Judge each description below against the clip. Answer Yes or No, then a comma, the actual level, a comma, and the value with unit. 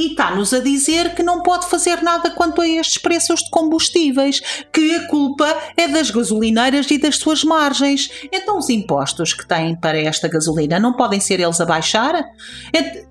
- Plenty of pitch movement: Yes, wide, 7.1 semitones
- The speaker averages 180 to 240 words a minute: Yes, fast, 185 wpm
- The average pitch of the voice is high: Yes, very high, 300 Hz